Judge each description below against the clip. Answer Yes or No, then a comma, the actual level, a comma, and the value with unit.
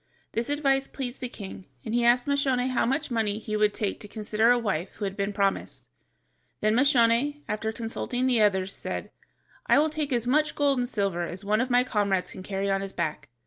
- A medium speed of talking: No, fast, 215 wpm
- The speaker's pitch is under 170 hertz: No, high, 230 Hz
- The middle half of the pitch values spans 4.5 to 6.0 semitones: No, average, 4.1 semitones